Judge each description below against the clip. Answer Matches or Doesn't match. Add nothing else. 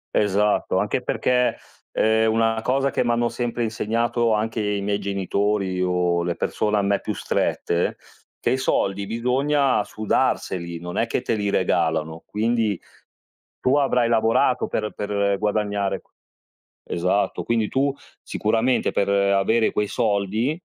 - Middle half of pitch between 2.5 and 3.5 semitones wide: Matches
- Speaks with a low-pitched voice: Matches